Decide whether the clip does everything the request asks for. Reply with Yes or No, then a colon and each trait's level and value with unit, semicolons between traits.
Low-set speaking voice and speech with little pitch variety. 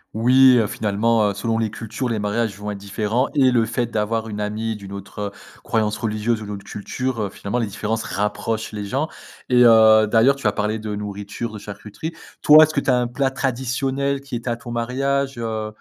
No: low, 115 Hz; average, 3.1 semitones